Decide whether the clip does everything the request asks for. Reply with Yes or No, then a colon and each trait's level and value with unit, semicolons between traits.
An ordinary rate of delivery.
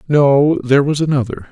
Yes: average, 160 wpm